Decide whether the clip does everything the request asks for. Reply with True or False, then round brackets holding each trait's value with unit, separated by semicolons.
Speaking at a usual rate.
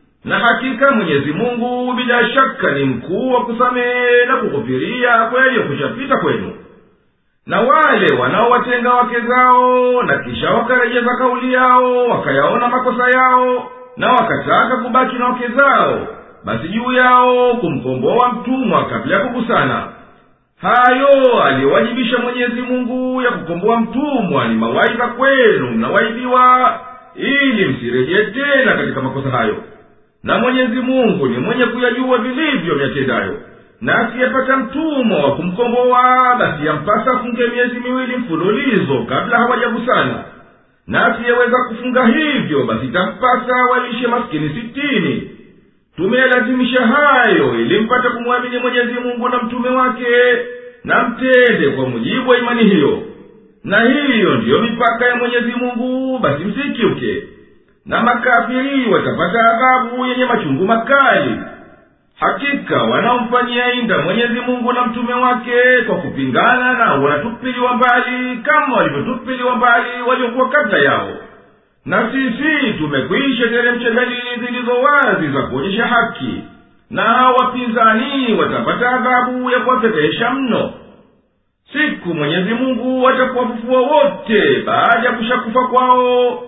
True (115 wpm)